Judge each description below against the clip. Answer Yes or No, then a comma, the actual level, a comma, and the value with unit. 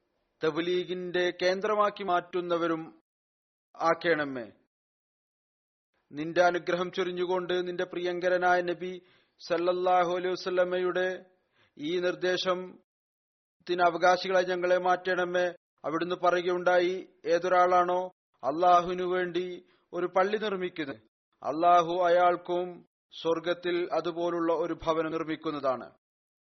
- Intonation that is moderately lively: No, narrow, 0.8 semitones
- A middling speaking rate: Yes, average, 70 wpm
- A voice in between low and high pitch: Yes, medium, 180 Hz